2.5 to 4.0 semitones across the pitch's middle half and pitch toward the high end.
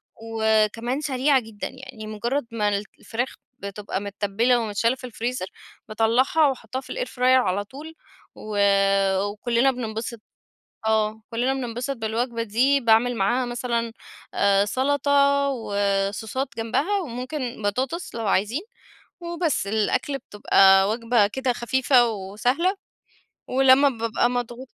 Yes: average, 3.3 semitones; high, 235 Hz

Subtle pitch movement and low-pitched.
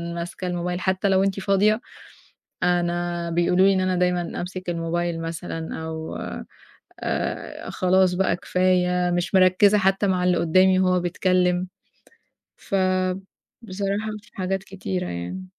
No: narrow, 1.3 semitones; medium, 185 Hz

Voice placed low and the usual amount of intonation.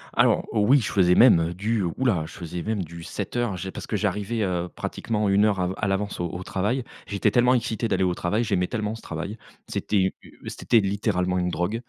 Yes: low, 100 Hz; average, 3.7 semitones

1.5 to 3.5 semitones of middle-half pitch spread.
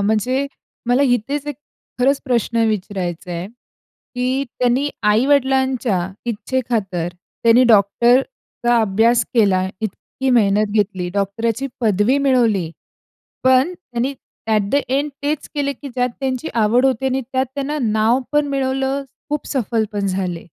No: average, 4.1 semitones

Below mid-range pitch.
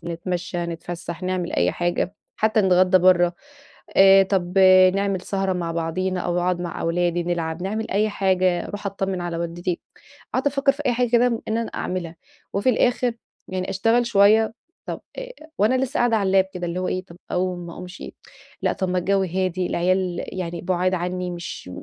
No: medium, 185 Hz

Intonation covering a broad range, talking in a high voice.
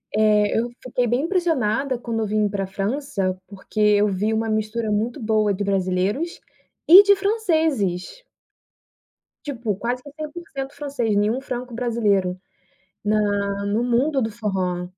No: average, 4.8 semitones; high, 220 Hz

